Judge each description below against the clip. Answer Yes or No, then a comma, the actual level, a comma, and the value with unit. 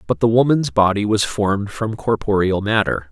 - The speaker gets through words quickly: No, average, 175 wpm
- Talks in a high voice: No, low, 105 Hz